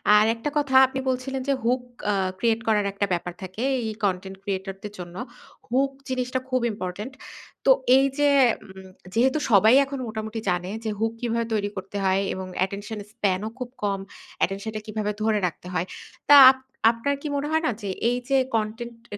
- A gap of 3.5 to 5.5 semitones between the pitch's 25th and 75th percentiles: Yes, average, 4.5 semitones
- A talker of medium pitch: No, high, 220 Hz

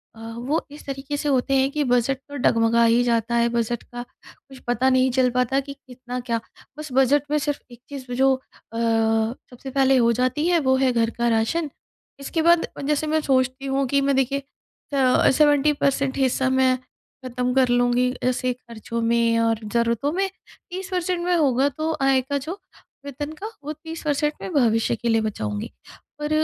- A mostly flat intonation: No, average, 3.1 semitones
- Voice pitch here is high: Yes, very high, 260 Hz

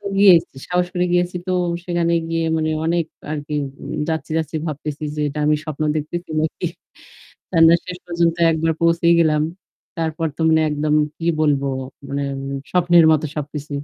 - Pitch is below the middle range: No, medium, 160 Hz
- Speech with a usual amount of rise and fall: No, narrow, 2.1 semitones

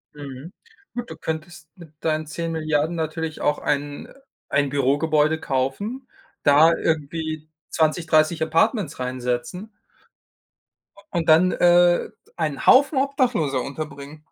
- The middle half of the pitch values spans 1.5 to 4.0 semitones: Yes, average, 2.9 semitones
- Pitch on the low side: No, medium, 155 Hz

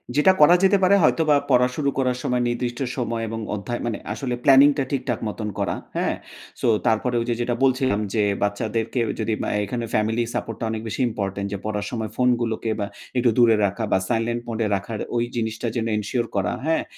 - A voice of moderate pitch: No, low, 120 Hz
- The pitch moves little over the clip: Yes, narrow, 2.3 semitones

